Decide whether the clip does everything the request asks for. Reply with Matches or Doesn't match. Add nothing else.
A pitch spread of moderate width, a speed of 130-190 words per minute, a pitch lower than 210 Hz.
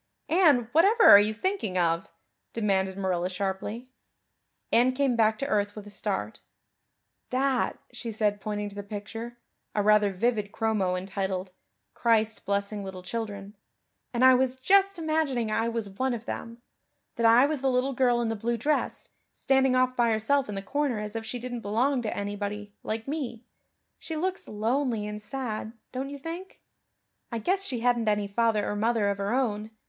Doesn't match